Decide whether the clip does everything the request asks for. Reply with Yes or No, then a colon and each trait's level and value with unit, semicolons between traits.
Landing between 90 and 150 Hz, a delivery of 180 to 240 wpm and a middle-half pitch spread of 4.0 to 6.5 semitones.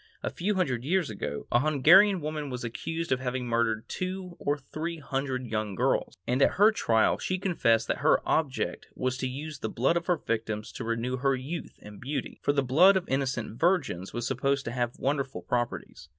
Yes: low, 135 Hz; average, 200 wpm; average, 5.2 semitones